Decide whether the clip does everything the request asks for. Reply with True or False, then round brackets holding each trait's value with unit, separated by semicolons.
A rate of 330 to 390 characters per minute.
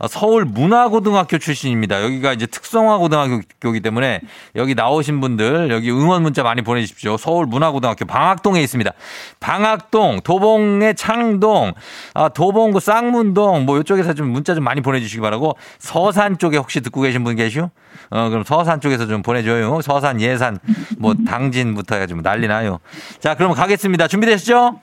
True (375 characters per minute)